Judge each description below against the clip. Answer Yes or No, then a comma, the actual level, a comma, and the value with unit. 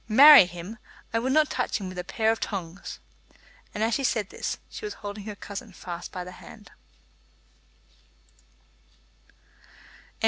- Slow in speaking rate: No, average, 145 wpm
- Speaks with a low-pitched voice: No, high, 210 Hz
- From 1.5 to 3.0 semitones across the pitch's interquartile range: No, average, 4.0 semitones